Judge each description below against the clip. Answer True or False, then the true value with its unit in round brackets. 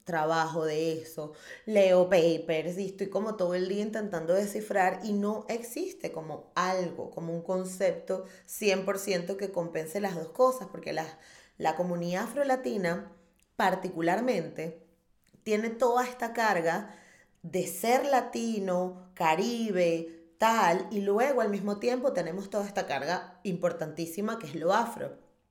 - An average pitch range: True (3.9 semitones)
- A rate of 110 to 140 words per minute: True (130 wpm)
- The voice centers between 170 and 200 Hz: True (185 Hz)